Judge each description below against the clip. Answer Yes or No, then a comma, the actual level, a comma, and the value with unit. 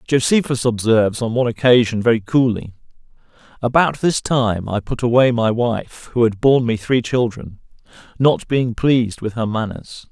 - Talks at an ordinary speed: Yes, average, 155 wpm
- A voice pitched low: Yes, low, 120 Hz